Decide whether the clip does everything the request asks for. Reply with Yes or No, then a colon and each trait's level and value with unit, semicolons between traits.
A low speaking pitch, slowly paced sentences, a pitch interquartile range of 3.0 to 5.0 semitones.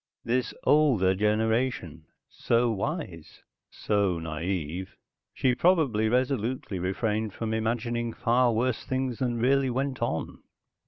Yes: low, 115 Hz; slow, 110 wpm; average, 4.1 semitones